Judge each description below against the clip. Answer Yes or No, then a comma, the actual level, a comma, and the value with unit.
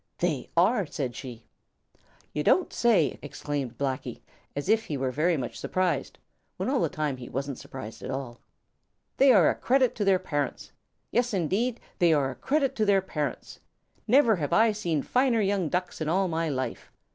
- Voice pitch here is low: No, medium, 170 Hz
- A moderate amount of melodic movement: No, wide, 7.3 semitones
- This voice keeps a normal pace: Yes, average, 185 wpm